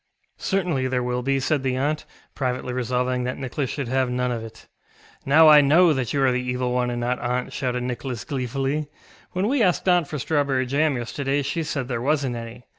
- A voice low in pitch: Yes, low, 130 Hz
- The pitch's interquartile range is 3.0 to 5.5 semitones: No, narrow, 2.6 semitones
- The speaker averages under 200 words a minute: No, fast, 205 wpm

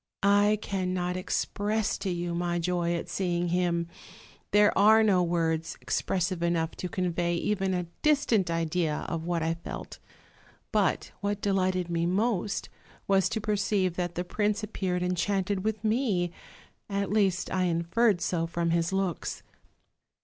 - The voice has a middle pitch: Yes, medium, 180 Hz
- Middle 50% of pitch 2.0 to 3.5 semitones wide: Yes, average, 2.8 semitones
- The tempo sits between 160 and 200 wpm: No, average, 145 wpm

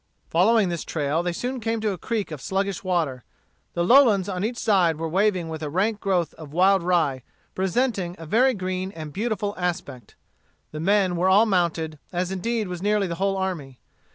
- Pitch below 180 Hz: No, medium, 185 Hz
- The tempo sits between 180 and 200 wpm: Yes, average, 190 wpm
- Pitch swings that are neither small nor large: Yes, average, 3.7 semitones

